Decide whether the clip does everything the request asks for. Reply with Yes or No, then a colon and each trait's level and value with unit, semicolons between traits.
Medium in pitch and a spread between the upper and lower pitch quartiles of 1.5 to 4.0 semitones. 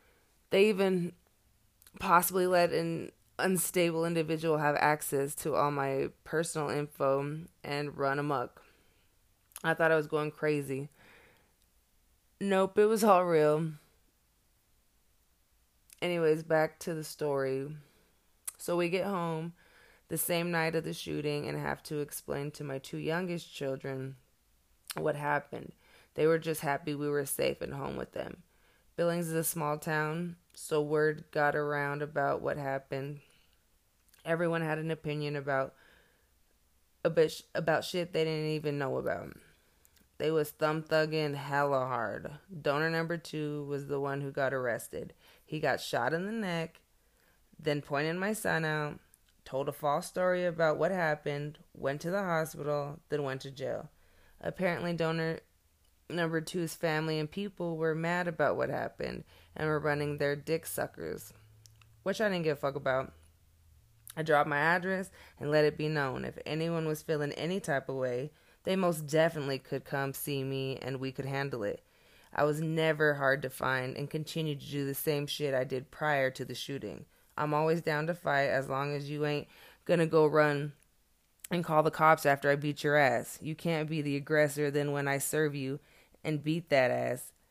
Yes: medium, 150 Hz; average, 2.8 semitones